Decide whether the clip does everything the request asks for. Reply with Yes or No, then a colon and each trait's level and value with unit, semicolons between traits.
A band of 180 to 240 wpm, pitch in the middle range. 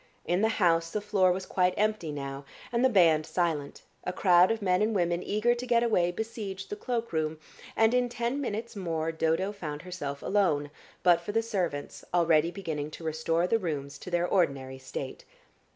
Yes: average, 185 wpm; medium, 180 Hz